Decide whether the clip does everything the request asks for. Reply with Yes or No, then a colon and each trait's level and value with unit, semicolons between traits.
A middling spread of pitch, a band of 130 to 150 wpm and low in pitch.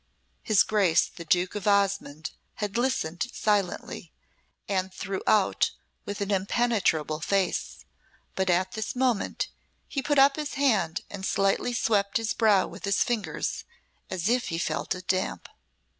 No: average, 3.2 semitones; average, 145 wpm; high, 200 Hz